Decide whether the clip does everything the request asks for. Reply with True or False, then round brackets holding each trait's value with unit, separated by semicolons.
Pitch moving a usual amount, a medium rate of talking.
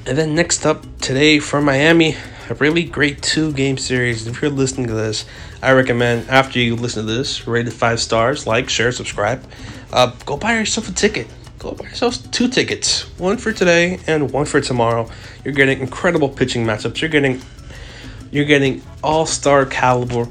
True (4.1 semitones; 175 wpm)